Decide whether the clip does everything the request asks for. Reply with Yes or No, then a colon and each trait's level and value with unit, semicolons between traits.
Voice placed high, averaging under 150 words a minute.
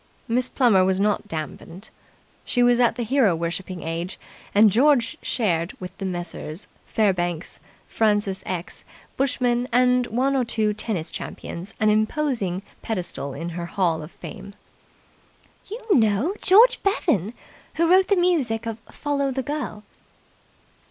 Yes: high, 215 Hz; average, 140 wpm